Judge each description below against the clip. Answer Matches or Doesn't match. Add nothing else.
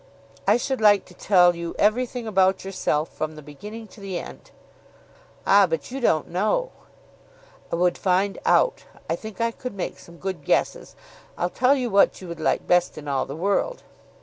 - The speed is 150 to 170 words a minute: Doesn't match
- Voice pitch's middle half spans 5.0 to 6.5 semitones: Doesn't match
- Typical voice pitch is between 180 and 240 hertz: Matches